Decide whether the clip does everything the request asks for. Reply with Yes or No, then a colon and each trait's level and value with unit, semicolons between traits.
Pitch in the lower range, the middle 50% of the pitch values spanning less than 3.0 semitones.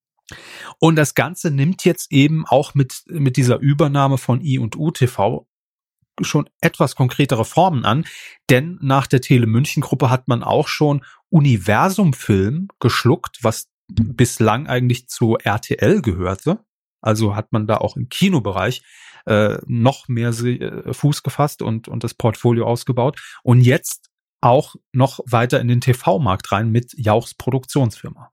No: low, 130 Hz; average, 4.1 semitones